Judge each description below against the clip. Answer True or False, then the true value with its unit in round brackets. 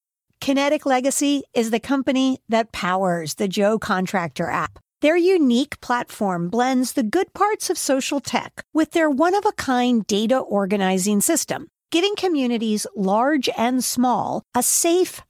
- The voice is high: True (255 Hz)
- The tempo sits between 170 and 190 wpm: False (145 wpm)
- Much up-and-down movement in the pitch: True (6.0 semitones)